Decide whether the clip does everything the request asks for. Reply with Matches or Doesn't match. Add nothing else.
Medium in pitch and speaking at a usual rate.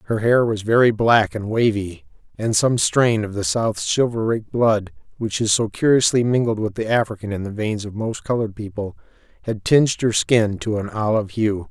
Doesn't match